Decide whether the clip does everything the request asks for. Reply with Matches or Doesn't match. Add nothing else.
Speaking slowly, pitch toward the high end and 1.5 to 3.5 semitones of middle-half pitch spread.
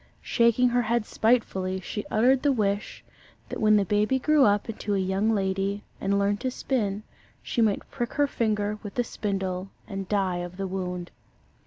Doesn't match